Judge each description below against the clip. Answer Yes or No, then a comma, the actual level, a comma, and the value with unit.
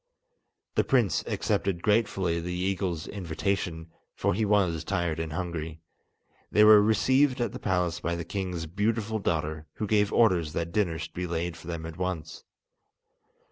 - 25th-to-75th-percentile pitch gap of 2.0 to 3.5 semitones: No, average, 3.9 semitones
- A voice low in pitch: Yes, very low, 90 Hz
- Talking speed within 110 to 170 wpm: Yes, average, 160 wpm